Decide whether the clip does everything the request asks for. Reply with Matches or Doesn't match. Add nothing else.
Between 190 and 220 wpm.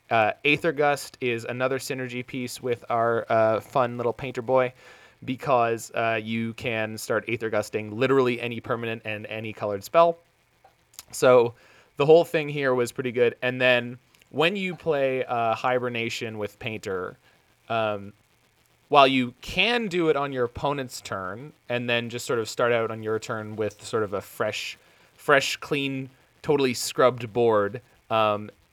Doesn't match